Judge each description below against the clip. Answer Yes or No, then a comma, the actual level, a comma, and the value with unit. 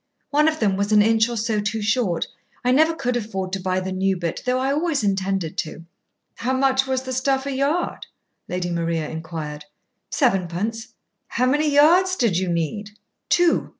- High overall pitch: Yes, high, 220 Hz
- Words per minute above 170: Yes, average, 185 wpm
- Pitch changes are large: Yes, wide, 6.2 semitones